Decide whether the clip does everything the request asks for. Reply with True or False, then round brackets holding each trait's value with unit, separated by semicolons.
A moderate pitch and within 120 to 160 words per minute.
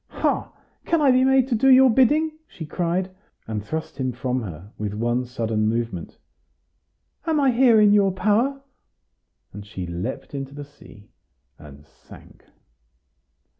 True (145 Hz; 150 wpm)